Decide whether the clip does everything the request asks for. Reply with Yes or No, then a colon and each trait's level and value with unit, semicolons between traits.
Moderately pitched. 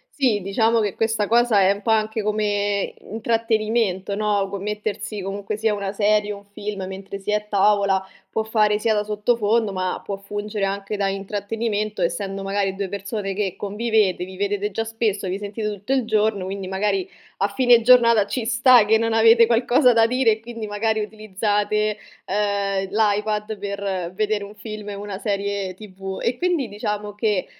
No: high, 210 Hz